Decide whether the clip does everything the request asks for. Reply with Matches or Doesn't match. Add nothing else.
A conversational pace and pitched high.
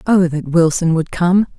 Doesn't match